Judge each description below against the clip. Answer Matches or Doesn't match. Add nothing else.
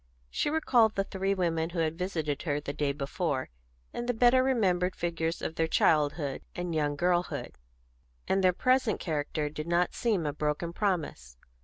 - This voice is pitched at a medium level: Matches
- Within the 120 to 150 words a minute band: Doesn't match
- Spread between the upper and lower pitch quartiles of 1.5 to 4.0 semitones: Doesn't match